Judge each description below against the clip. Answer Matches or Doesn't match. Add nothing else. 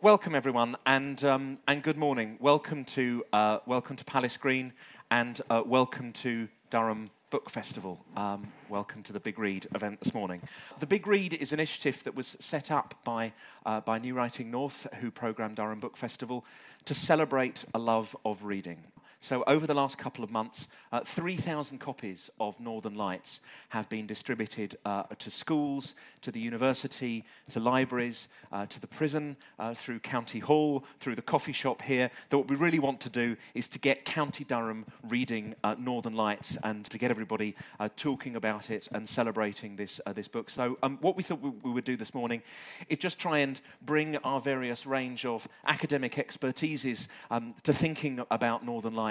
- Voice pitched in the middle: Doesn't match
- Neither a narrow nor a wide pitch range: Matches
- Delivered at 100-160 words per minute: Doesn't match